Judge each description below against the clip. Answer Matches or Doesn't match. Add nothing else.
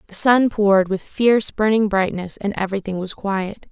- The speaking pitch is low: Doesn't match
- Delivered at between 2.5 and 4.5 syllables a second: Doesn't match